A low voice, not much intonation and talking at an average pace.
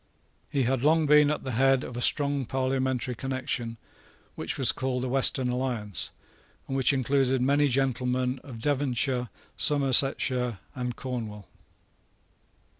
No: low, 130 Hz; narrow, 1.6 semitones; slow, 130 wpm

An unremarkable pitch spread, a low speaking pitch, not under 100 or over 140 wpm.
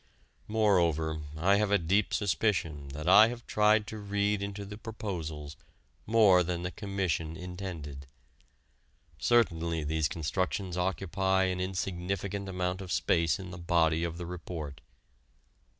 Yes: average, 3.6 semitones; very low, 90 Hz; slow, 135 wpm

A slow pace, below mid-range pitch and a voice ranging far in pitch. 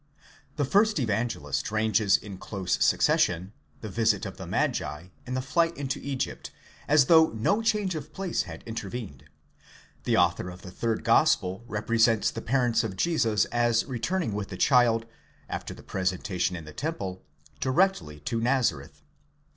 No: average, 155 wpm; low, 115 Hz; wide, 6.1 semitones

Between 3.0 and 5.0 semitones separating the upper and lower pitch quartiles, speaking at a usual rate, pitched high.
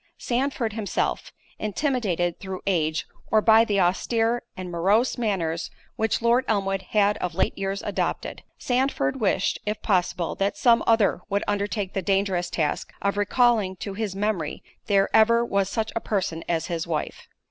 Yes: average, 3.3 semitones; average, 160 wpm; high, 200 Hz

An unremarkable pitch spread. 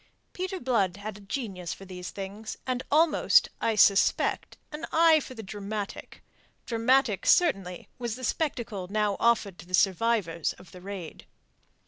Yes: average, 4.7 semitones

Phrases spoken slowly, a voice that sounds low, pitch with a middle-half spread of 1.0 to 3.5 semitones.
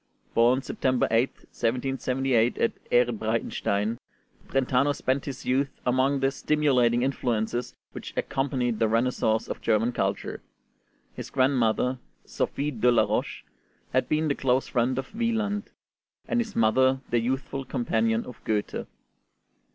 Yes: slow, 130 wpm; low, 125 Hz; narrow, 2.5 semitones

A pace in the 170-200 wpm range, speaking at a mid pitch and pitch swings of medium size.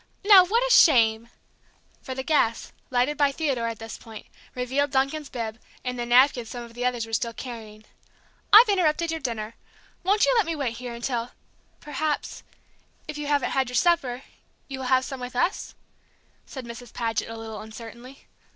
No: average, 185 wpm; very high, 250 Hz; average, 4.2 semitones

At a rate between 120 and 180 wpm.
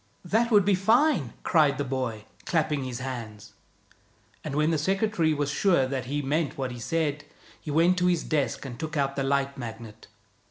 No: average, 190 wpm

